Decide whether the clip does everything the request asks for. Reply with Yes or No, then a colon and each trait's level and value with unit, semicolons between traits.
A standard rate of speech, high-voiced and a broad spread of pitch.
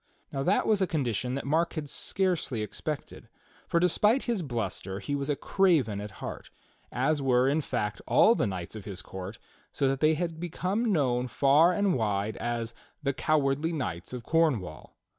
No: average, 180 wpm; medium, 140 Hz; wide, 6.7 semitones